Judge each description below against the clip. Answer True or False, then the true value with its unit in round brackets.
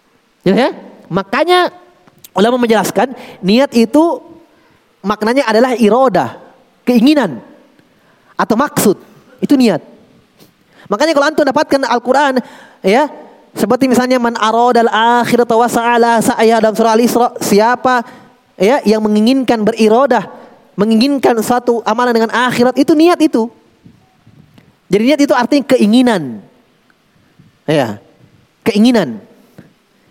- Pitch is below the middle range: False (240 Hz)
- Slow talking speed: False (100 wpm)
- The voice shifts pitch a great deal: False (2.9 semitones)